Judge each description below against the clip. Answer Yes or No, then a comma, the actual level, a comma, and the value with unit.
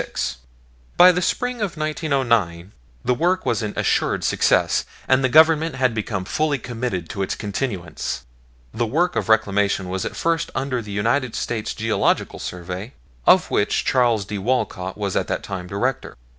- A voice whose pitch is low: Yes, low, 115 Hz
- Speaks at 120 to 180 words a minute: Yes, average, 160 wpm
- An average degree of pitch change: No, wide, 6.0 semitones